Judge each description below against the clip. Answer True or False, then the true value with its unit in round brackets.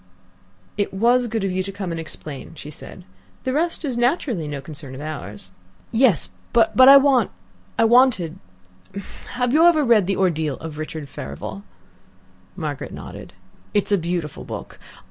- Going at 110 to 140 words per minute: False (160 wpm)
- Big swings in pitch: True (7.9 semitones)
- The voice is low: False (190 Hz)